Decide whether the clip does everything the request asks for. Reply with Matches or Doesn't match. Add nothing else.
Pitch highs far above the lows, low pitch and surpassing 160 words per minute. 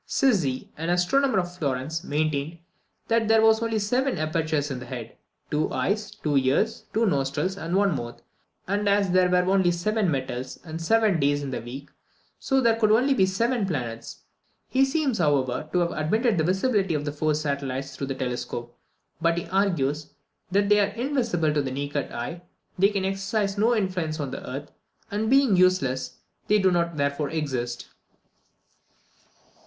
Doesn't match